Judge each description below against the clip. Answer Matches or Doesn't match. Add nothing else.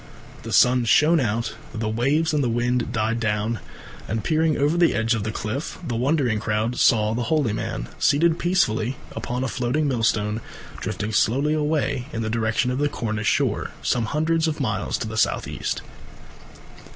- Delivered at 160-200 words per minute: Matches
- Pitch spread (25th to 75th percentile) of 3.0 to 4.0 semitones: Doesn't match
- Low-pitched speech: Matches